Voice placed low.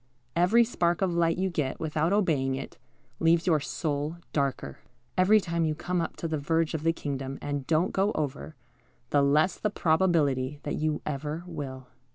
No: medium, 160 Hz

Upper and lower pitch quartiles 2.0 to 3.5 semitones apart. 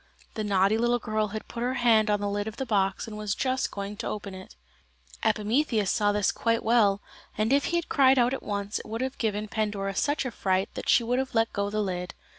Yes: average, 2.9 semitones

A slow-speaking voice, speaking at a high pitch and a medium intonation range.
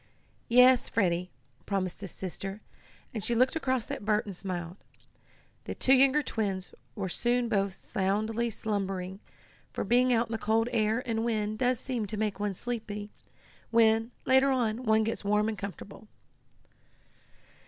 No: average, 155 wpm; high, 220 Hz; average, 3.0 semitones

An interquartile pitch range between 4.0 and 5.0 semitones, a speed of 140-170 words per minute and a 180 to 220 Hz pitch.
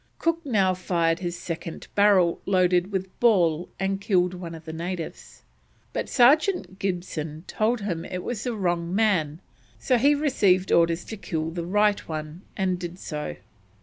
No: average, 3.5 semitones; average, 160 wpm; medium, 185 Hz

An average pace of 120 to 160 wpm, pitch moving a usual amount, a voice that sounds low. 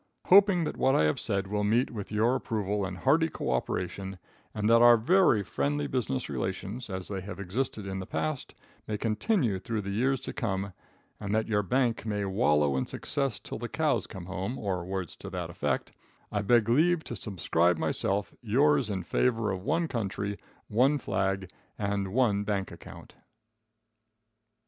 No: average, 175 wpm; average, 4.5 semitones; low, 105 Hz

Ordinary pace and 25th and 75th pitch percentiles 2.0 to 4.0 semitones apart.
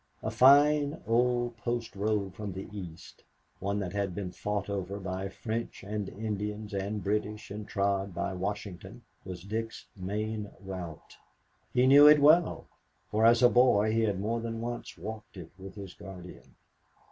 Yes: average, 160 wpm; average, 2.8 semitones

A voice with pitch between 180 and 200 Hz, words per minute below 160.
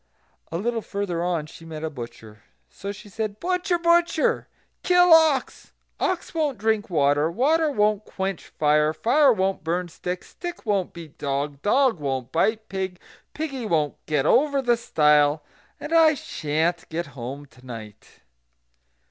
Yes: high, 190 Hz; average, 150 wpm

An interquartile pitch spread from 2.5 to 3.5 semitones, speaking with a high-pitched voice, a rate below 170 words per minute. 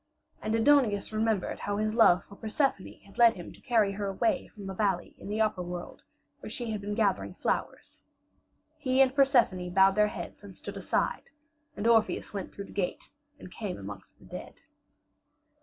No: average, 2.9 semitones; high, 210 Hz; average, 185 wpm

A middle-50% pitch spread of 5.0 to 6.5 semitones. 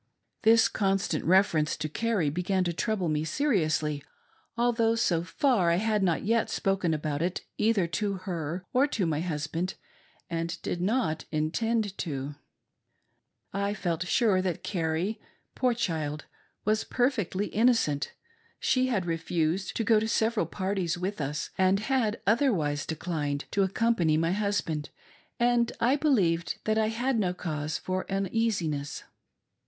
Yes: wide, 5.4 semitones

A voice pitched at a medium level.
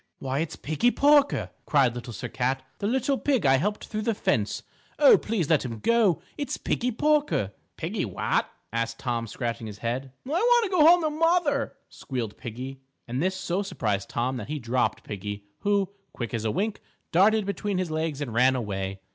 Yes: medium, 155 Hz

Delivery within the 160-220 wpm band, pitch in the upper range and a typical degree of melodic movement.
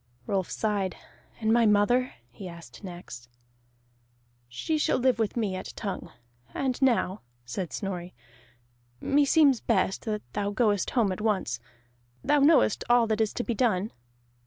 No: average, 145 wpm; high, 210 Hz; average, 4.4 semitones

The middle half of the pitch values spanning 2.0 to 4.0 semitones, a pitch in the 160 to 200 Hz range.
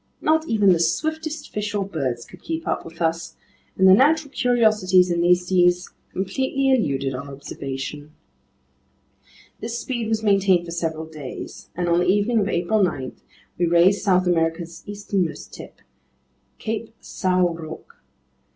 No: average, 4.7 semitones; medium, 185 Hz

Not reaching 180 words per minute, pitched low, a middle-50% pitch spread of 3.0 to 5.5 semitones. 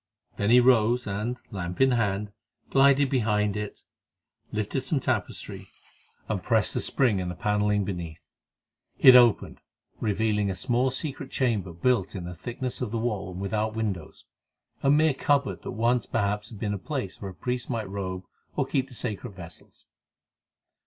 Yes: average, 165 wpm; low, 110 Hz; average, 4.2 semitones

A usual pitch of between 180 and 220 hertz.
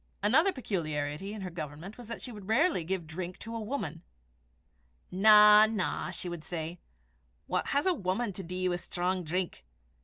Yes: medium, 185 Hz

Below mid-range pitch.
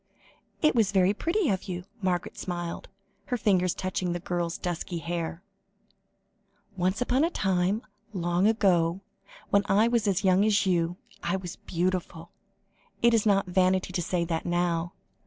No: medium, 185 Hz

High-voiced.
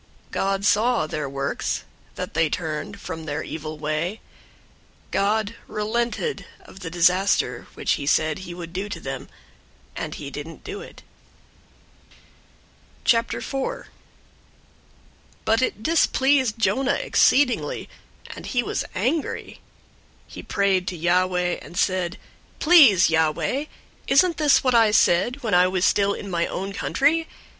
Yes: high, 195 Hz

